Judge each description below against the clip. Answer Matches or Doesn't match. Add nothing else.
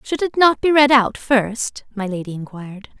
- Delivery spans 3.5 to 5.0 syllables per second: Matches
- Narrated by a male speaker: Doesn't match